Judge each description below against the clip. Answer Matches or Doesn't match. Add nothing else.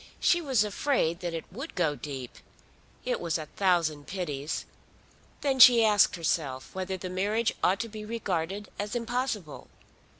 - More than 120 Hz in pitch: Matches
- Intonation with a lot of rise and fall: Matches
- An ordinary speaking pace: Matches